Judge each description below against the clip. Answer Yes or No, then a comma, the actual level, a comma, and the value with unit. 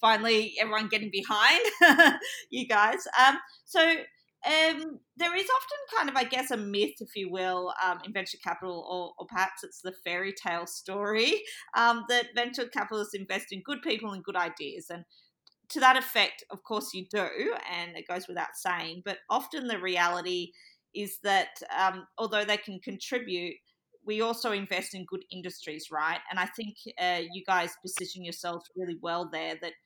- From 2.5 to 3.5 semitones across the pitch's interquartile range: No, average, 4.5 semitones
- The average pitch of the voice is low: No, high, 195 Hz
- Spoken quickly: No, average, 175 wpm